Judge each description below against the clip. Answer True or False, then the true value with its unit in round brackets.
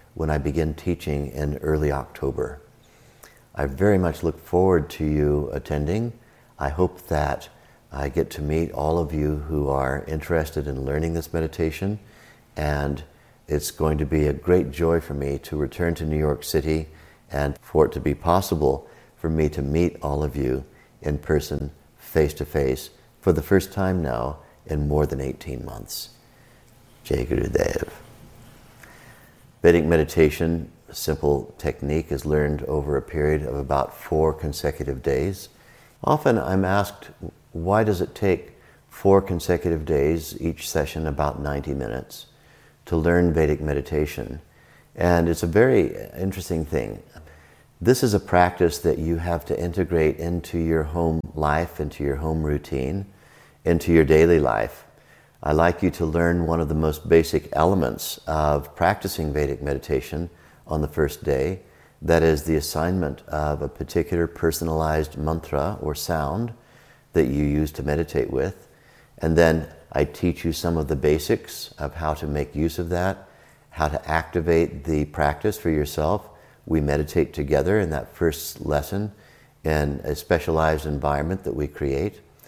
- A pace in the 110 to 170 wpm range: True (155 wpm)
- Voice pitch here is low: True (80 Hz)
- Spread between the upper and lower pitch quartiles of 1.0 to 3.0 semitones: True (2.7 semitones)